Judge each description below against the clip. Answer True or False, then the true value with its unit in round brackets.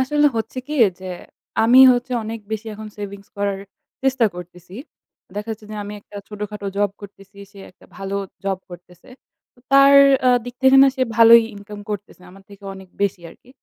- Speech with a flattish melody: False (3.5 semitones)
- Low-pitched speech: False (210 Hz)